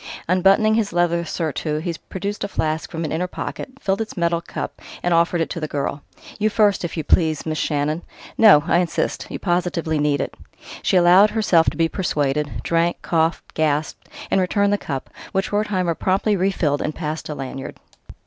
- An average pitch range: Yes, average, 3.6 semitones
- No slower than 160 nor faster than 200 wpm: Yes, average, 185 wpm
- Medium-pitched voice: Yes, medium, 170 Hz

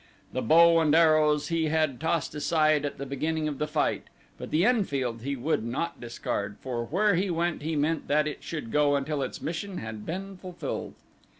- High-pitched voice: No, medium, 155 Hz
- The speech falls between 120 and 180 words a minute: No, average, 195 wpm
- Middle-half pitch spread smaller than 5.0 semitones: Yes, average, 3.1 semitones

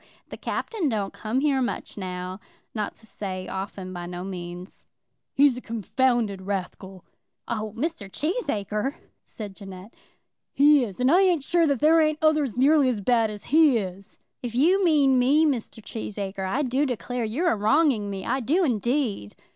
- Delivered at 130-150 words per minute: No, average, 170 wpm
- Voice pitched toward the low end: No, high, 235 Hz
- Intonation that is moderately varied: No, wide, 6.5 semitones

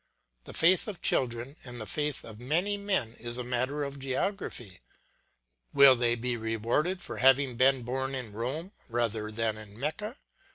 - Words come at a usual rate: Yes, average, 165 wpm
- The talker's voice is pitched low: Yes, low, 125 Hz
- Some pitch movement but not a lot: Yes, average, 4.1 semitones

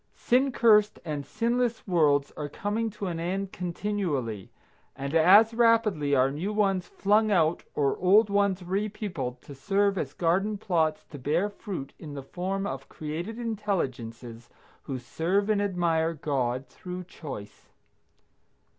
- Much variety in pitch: Yes, wide, 6.0 semitones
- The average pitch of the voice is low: No, medium, 180 Hz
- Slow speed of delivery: No, average, 145 wpm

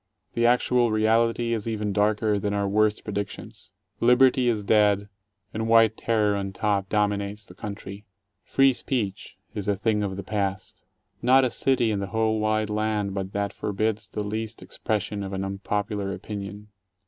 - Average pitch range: No, narrow, 1.8 semitones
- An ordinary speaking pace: Yes, average, 170 wpm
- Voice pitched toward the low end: Yes, low, 105 Hz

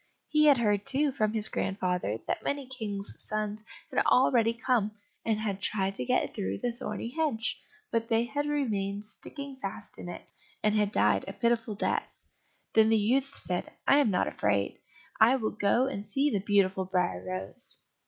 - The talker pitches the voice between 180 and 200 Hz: No, high, 220 Hz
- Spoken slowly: No, average, 180 wpm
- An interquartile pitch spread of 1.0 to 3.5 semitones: No, average, 4.4 semitones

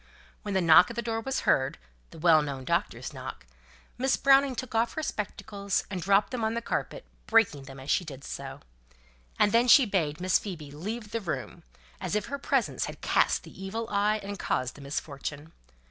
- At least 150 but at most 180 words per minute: No, average, 200 wpm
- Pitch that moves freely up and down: Yes, wide, 6.6 semitones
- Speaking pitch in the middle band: No, high, 200 Hz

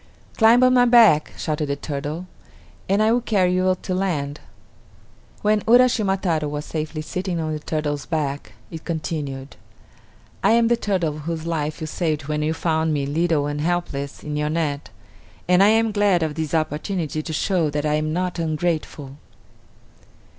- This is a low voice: No, medium, 160 Hz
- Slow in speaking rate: No, average, 170 wpm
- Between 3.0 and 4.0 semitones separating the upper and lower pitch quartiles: Yes, average, 3.7 semitones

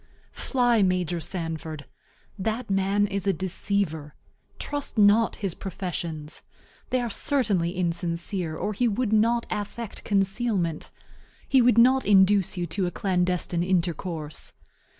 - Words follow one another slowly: Yes, slow, 125 wpm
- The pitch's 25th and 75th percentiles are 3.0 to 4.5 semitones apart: Yes, average, 3.9 semitones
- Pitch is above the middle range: Yes, high, 195 Hz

